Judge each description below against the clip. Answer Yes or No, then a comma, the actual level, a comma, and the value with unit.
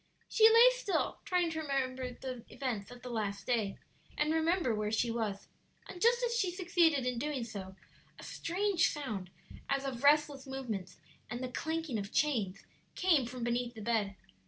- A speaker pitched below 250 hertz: No, very high, 260 Hz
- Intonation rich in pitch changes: Yes, wide, 6.1 semitones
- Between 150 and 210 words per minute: Yes, average, 175 wpm